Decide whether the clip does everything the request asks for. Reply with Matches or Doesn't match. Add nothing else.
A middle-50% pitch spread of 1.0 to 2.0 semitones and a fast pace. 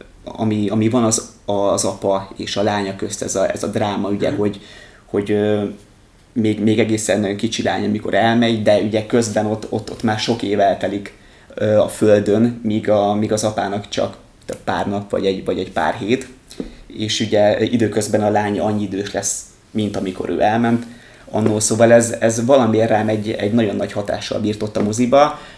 Matches